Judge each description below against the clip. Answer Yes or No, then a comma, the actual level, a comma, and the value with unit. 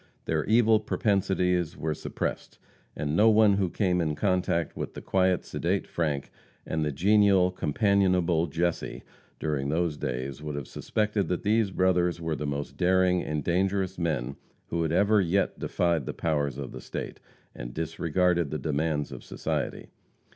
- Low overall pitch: Yes, very low, 85 Hz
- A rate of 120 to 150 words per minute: No, average, 160 wpm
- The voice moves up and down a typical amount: Yes, average, 3.9 semitones